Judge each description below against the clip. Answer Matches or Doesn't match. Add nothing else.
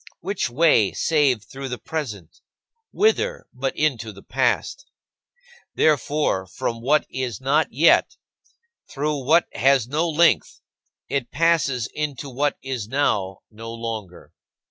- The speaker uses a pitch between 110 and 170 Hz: Matches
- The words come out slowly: Matches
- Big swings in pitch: Doesn't match